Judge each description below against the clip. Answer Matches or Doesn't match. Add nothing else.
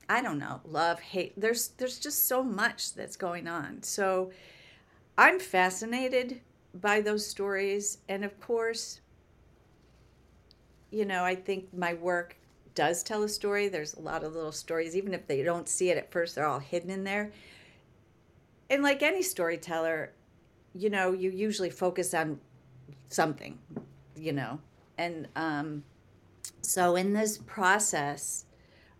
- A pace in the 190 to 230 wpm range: Doesn't match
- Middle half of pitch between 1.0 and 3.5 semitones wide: Doesn't match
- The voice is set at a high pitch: Doesn't match